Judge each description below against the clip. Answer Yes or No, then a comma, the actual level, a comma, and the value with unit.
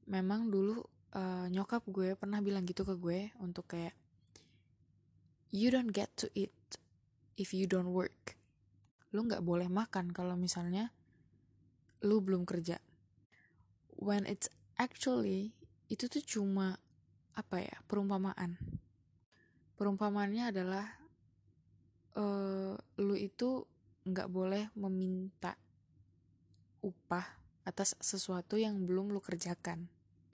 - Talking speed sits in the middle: Yes, average, 105 wpm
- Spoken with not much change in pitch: Yes, narrow, 2.2 semitones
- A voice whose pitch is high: Yes, high, 195 Hz